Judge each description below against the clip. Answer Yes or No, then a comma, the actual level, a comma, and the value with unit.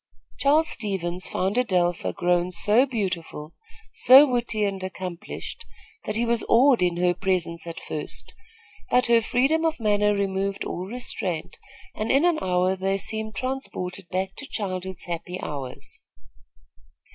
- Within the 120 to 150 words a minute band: Yes, average, 140 wpm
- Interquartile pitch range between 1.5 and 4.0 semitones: No, average, 4.7 semitones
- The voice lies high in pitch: Yes, high, 195 Hz